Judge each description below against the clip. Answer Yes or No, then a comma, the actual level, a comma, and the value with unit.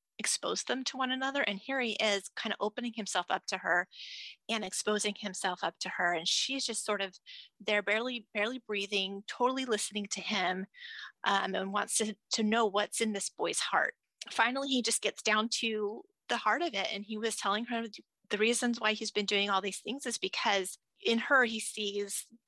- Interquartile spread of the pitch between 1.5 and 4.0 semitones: Yes, narrow, 2.5 semitones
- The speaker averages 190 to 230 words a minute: Yes, fast, 205 wpm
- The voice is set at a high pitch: Yes, high, 215 Hz